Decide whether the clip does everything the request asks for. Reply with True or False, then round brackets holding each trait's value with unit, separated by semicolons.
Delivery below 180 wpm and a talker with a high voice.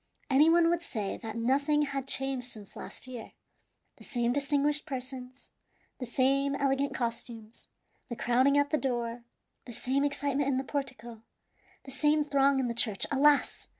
True (160 wpm; 270 Hz)